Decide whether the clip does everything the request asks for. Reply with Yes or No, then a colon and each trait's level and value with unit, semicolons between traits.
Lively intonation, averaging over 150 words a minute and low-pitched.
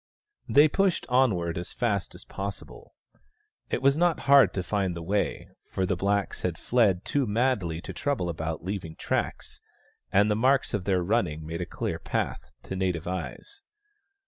Yes: wide, 6.1 semitones; average, 170 wpm; low, 100 Hz